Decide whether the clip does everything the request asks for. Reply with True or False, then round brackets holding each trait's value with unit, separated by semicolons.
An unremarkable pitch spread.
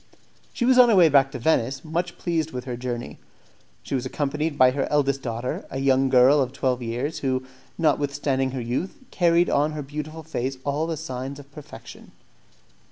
True (3.1 semitones)